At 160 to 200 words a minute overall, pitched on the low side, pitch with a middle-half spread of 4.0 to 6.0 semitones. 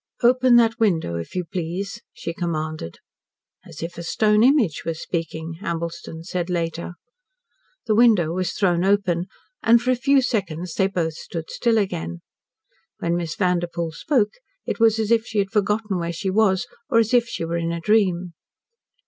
No: average, 175 wpm; medium, 180 Hz; average, 4.7 semitones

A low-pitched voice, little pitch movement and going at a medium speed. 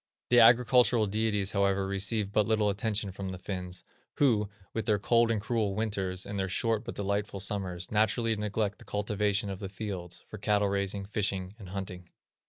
Yes: low, 100 Hz; narrow, 2.0 semitones; average, 180 wpm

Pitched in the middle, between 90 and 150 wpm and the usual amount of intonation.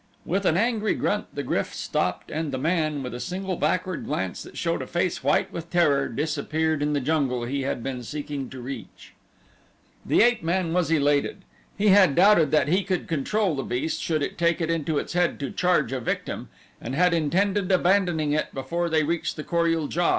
No: medium, 160 Hz; fast, 205 wpm; average, 4.0 semitones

